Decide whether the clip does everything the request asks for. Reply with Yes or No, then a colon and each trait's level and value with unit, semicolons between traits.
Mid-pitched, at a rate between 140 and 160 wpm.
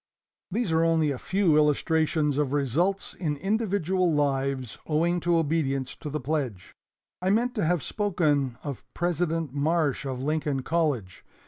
Yes: medium, 155 Hz; average, 145 wpm